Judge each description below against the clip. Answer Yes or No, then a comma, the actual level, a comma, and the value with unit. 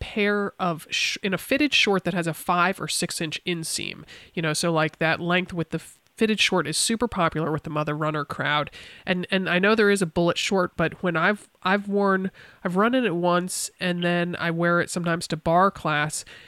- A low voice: No, medium, 175 Hz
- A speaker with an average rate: No, fast, 220 wpm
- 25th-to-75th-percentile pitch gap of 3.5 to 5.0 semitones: No, average, 2.9 semitones